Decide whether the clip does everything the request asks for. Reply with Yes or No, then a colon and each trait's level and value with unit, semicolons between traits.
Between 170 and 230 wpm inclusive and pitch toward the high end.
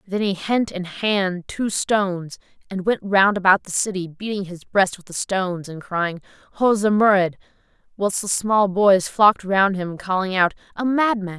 Yes: average, 180 wpm; high, 195 Hz